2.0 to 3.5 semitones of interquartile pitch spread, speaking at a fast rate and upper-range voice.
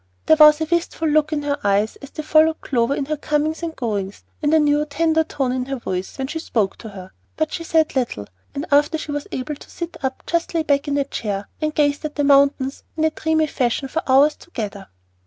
Yes: average, 3.2 semitones; fast, 235 wpm; very high, 290 Hz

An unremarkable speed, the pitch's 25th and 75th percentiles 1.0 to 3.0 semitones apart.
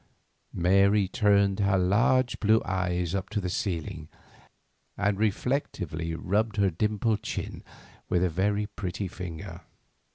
No: slow, 125 wpm; narrow, 2.5 semitones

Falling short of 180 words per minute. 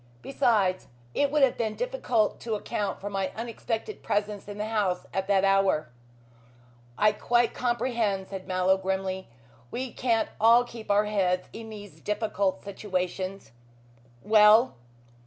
Yes: average, 140 wpm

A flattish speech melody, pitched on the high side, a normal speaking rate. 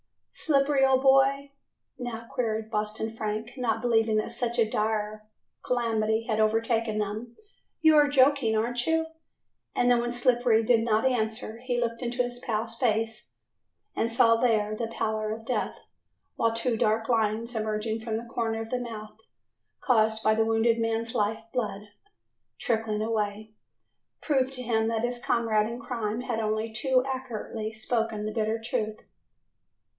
Yes: narrow, 1.9 semitones; high, 225 Hz; average, 155 wpm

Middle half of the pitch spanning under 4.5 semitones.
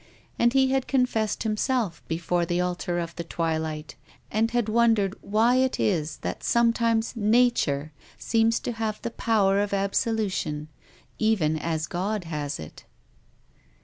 No: wide, 5.4 semitones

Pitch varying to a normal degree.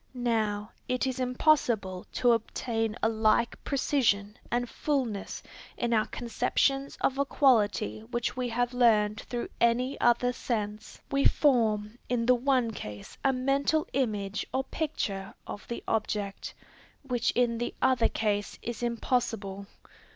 Yes: average, 3.0 semitones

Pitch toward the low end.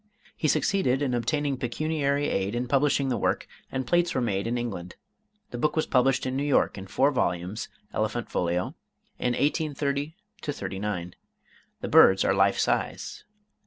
Yes: low, 130 Hz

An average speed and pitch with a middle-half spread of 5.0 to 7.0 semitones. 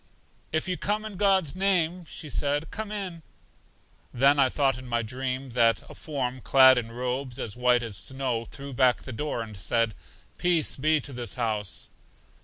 No: average, 180 wpm; average, 4.5 semitones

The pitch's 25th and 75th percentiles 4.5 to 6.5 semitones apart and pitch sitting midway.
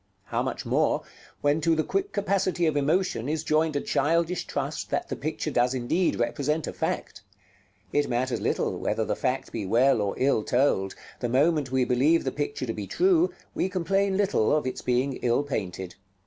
Yes: average, 5.1 semitones; medium, 145 Hz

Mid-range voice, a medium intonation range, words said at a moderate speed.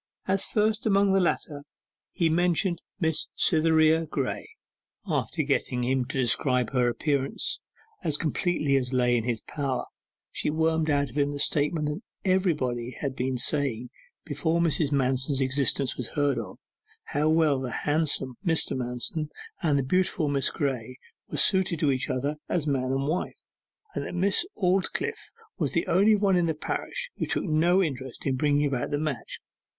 Yes: medium, 145 Hz; average, 4.1 semitones; average, 165 wpm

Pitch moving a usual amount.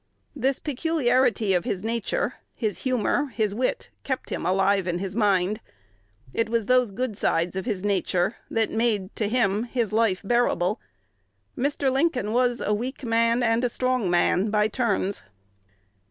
Yes: average, 3.9 semitones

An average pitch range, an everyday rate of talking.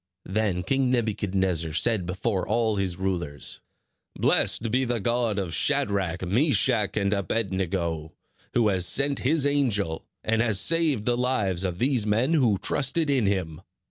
Yes: average, 5.0 semitones; average, 150 wpm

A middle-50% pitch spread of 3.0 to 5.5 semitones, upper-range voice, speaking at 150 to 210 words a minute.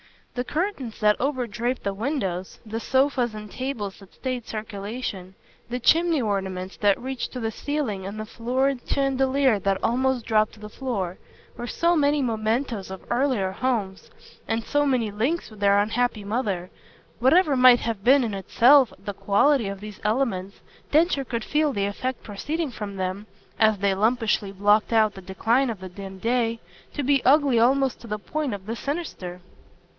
Yes: average, 4.6 semitones; high, 230 Hz; average, 170 wpm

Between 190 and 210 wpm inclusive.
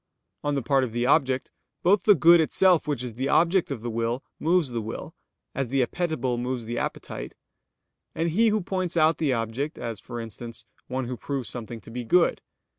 Yes: average, 200 wpm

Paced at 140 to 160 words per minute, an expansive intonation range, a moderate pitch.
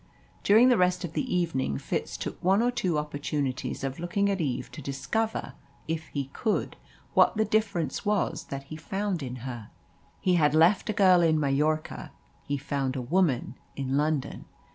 No: average, 175 wpm; wide, 5.7 semitones; medium, 160 Hz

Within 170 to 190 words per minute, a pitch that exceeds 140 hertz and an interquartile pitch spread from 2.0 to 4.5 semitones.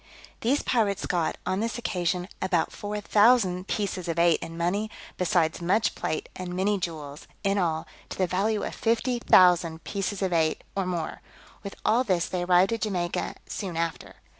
Yes: average, 175 wpm; medium, 185 Hz; average, 3.1 semitones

